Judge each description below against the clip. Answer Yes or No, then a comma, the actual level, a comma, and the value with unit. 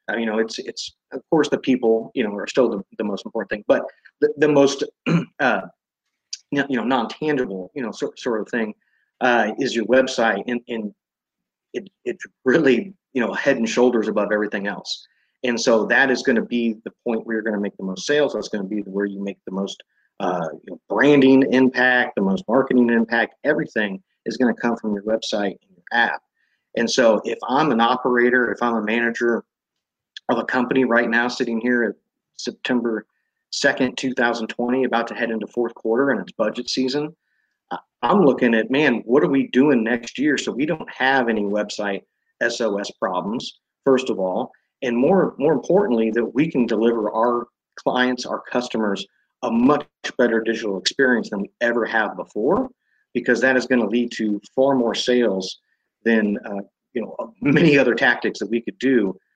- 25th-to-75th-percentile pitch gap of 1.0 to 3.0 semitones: Yes, narrow, 2.6 semitones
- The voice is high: No, low, 120 Hz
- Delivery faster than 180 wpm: Yes, average, 195 wpm